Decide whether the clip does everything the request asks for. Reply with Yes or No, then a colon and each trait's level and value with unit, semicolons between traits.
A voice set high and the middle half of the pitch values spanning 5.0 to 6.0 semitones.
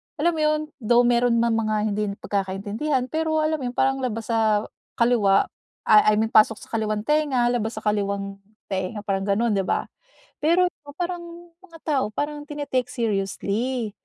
Yes: high, 235 Hz; wide, 5.5 semitones